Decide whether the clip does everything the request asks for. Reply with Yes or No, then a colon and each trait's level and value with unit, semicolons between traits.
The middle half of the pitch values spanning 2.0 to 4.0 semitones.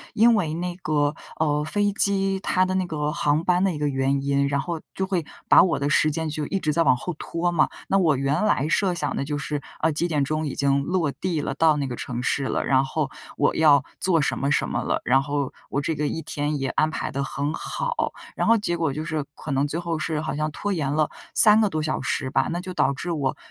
Yes: average, 3.6 semitones